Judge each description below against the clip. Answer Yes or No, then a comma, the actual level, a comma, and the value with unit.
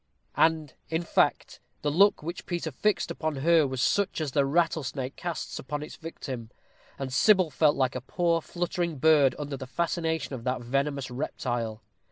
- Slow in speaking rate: No, average, 170 wpm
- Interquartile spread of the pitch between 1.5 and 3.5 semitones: No, average, 4.0 semitones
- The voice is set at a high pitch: No, medium, 150 Hz